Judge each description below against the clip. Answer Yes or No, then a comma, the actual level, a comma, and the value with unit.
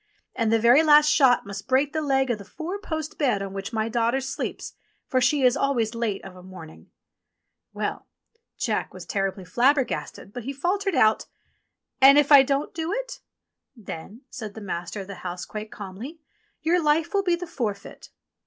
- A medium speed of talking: Yes, average, 190 wpm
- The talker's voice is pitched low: No, very high, 250 Hz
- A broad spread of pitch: Yes, wide, 6.4 semitones